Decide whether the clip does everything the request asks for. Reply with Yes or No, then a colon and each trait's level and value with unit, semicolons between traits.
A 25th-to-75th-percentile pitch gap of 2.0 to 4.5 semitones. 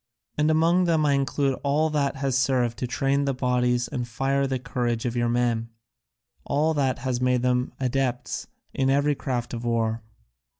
Yes: narrow, 2.4 semitones